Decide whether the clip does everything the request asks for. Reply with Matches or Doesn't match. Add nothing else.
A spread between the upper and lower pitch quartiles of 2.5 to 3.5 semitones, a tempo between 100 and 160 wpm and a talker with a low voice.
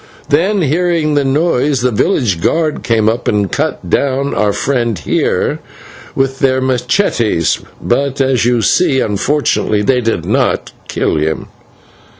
Doesn't match